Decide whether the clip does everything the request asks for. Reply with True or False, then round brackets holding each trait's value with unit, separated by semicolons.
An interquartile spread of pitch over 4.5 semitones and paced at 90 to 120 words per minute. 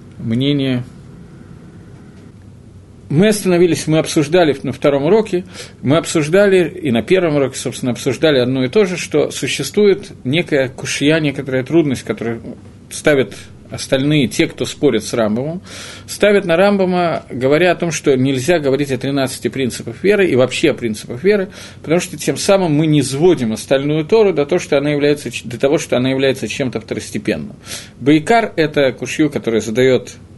False (5.5 semitones; 150 wpm)